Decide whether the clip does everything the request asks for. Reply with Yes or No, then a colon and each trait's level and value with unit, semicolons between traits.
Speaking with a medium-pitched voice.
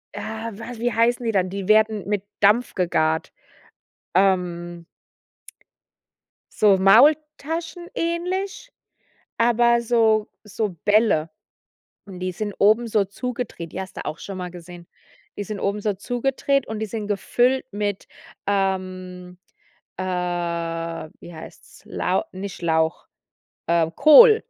No: high, 205 Hz